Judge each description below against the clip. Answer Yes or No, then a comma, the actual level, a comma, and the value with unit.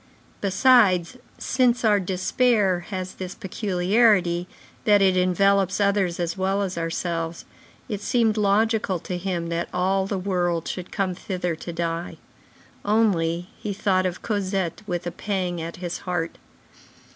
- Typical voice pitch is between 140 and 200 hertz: Yes, medium, 185 Hz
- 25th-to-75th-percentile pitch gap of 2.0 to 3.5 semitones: Yes, narrow, 2.5 semitones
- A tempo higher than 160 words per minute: No, average, 140 wpm